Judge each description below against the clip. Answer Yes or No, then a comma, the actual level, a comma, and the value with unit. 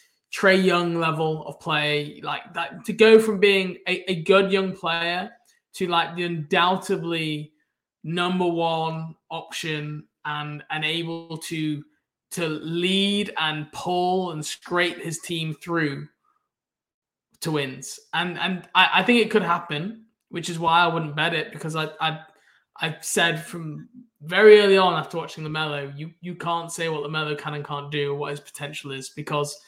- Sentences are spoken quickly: No, average, 170 wpm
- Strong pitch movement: No, average, 2.9 semitones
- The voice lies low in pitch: No, medium, 165 Hz